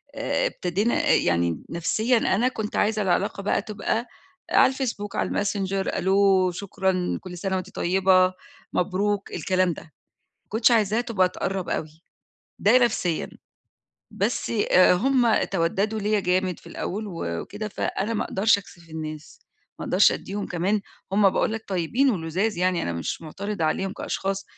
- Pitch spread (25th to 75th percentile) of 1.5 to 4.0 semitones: Yes, average, 2.9 semitones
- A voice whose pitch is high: Yes, high, 195 Hz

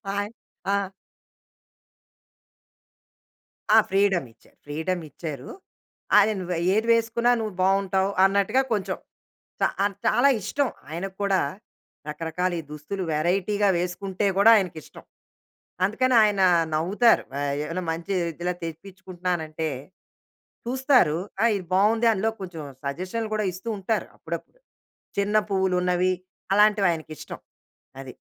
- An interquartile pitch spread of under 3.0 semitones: No, average, 3.5 semitones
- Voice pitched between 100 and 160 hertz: No, high, 190 Hz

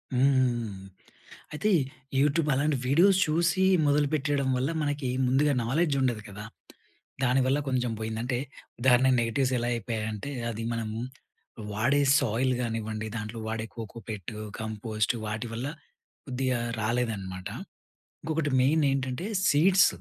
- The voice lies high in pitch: No, low, 125 Hz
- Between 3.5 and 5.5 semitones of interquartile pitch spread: Yes, average, 4.2 semitones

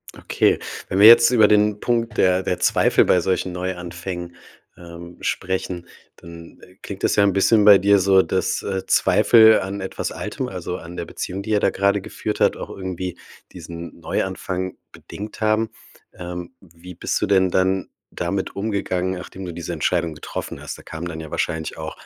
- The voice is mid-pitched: No, very low, 95 Hz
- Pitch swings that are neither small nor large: No, narrow, 2.3 semitones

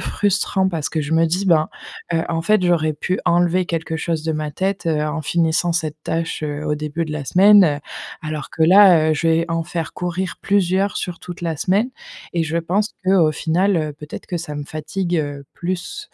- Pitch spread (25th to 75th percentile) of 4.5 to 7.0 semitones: No, average, 2.7 semitones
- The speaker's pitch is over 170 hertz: No, medium, 165 Hz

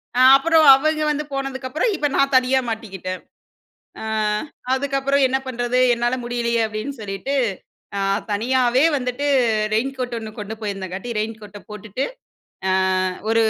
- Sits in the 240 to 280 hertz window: Yes, high, 245 Hz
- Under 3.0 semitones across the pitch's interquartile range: No, average, 3.8 semitones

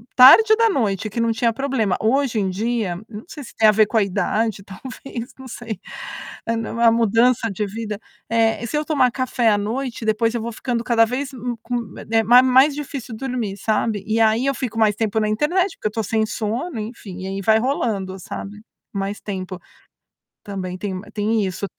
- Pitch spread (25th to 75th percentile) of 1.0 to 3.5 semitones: Yes, average, 3.1 semitones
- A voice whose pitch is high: Yes, high, 225 Hz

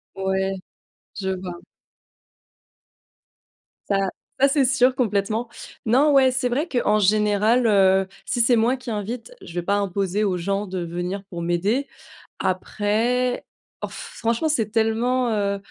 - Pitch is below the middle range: No, high, 210 Hz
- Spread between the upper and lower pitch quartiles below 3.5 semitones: No, average, 4.2 semitones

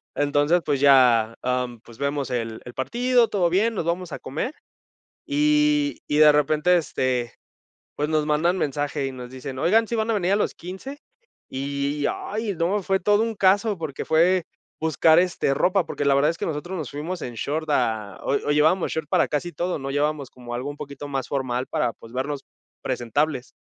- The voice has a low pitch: No, medium, 150 Hz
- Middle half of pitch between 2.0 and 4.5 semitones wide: No, average, 5.2 semitones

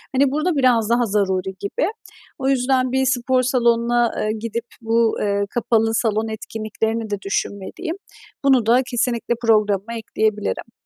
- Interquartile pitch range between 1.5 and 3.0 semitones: Yes, average, 2.7 semitones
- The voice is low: No, high, 230 Hz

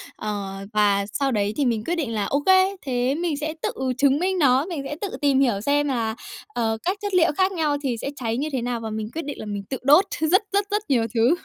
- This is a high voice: Yes, very high, 275 Hz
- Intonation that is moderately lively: No, wide, 6.1 semitones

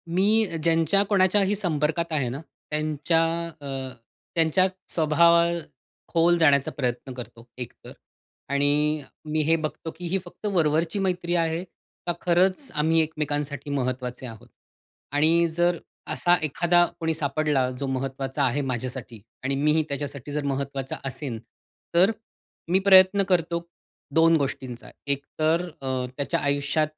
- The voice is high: No, medium, 155 Hz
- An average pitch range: Yes, average, 3.6 semitones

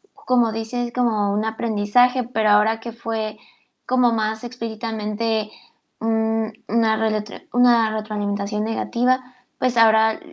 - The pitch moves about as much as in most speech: No, narrow, 1.6 semitones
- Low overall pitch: No, high, 225 Hz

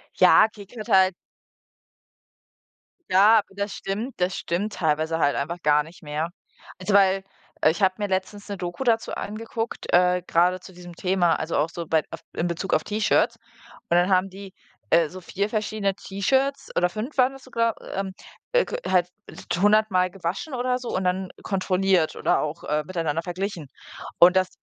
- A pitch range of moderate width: Yes, average, 3.2 semitones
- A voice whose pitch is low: No, medium, 185 Hz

